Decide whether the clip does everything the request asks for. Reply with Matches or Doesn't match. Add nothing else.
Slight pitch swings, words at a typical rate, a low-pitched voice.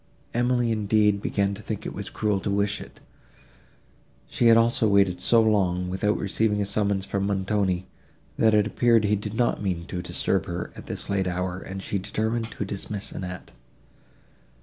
Matches